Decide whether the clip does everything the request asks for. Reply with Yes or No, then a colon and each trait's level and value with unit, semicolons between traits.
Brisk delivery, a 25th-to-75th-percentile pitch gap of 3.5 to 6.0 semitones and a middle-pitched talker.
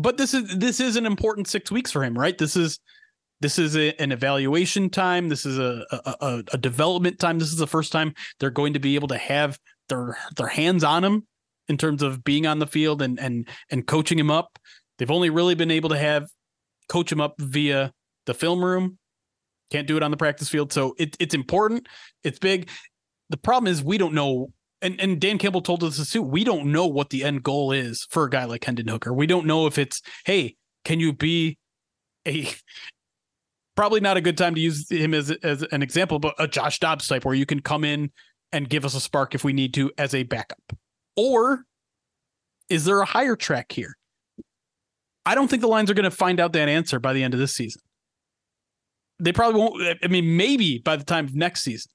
Yes: fast, 225 wpm; average, 4.1 semitones; medium, 155 Hz